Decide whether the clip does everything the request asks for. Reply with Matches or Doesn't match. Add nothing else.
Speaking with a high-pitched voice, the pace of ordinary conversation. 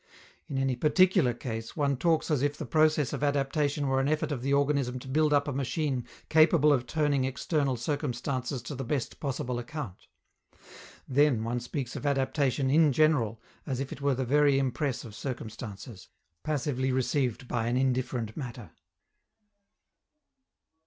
Doesn't match